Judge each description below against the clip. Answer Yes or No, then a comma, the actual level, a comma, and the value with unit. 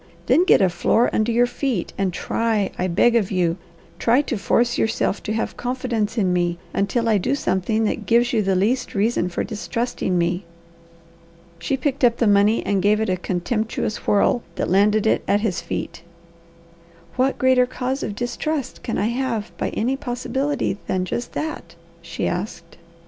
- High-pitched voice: Yes, high, 220 Hz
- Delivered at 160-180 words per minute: Yes, average, 175 wpm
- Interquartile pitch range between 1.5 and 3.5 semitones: No, average, 4.2 semitones